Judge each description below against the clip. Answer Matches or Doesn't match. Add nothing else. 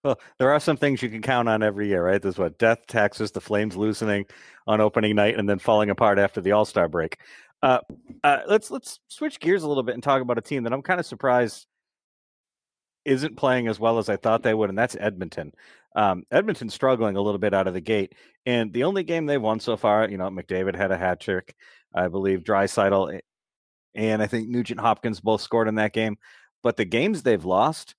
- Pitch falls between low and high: Doesn't match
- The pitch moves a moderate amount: Matches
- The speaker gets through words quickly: Matches